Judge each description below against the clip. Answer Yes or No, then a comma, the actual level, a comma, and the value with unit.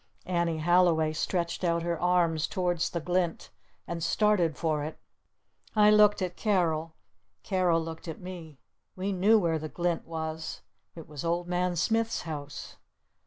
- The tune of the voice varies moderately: No, narrow, 2.1 semitones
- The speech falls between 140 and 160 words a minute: Yes, average, 150 wpm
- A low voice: No, medium, 170 Hz